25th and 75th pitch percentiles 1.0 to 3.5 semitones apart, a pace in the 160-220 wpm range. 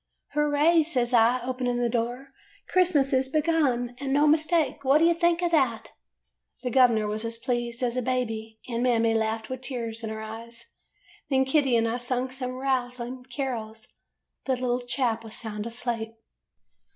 Yes: average, 2.8 semitones; average, 175 wpm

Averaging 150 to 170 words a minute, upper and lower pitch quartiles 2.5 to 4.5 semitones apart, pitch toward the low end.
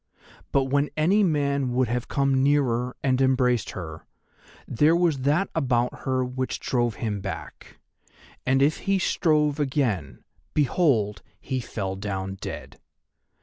No: slow, 135 wpm; average, 4.0 semitones; low, 130 Hz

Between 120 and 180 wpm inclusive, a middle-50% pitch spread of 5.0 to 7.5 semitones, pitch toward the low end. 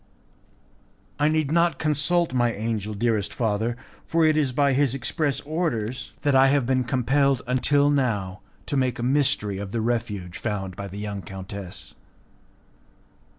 Yes: average, 150 wpm; wide, 5.4 semitones; low, 125 Hz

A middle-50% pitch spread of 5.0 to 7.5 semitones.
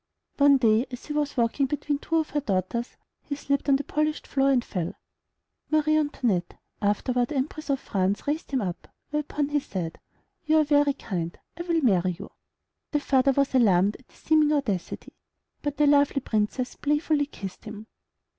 Yes: wide, 5.4 semitones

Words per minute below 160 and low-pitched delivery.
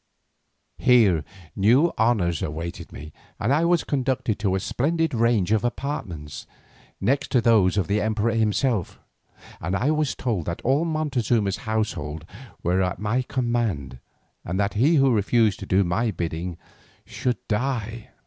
Yes: average, 150 wpm; low, 110 Hz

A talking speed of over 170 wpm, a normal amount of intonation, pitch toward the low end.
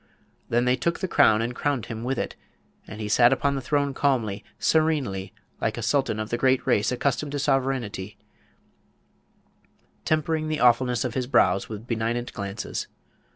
No: average, 165 wpm; average, 4.1 semitones; low, 125 Hz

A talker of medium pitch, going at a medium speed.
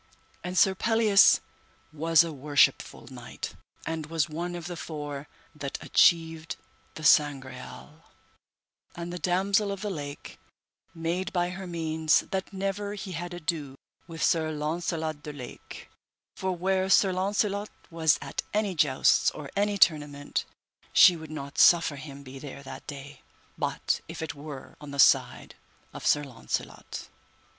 Yes: medium, 165 Hz; average, 145 wpm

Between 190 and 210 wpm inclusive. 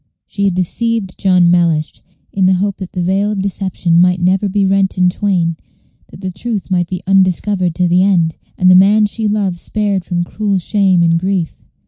Yes: average, 195 wpm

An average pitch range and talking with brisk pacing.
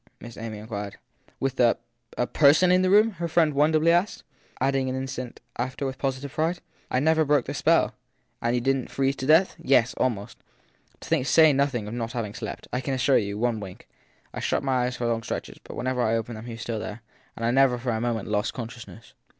Yes: average, 3.4 semitones; fast, 225 wpm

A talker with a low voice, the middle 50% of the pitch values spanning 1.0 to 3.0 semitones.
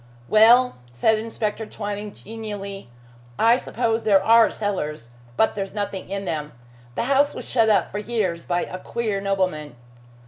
No: high, 205 Hz; average, 2.7 semitones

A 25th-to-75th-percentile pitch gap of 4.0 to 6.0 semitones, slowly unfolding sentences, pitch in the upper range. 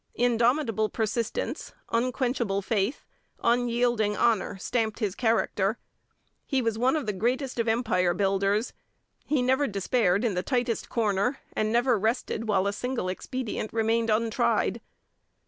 No: average, 2.9 semitones; slow, 130 wpm; high, 230 Hz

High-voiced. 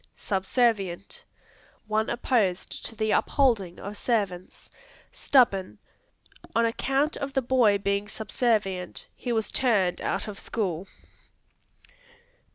Yes: high, 215 Hz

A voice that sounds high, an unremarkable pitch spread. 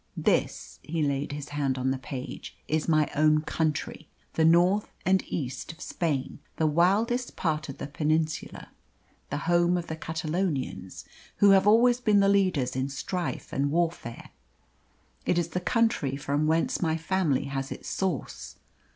No: medium, 160 Hz; average, 4.1 semitones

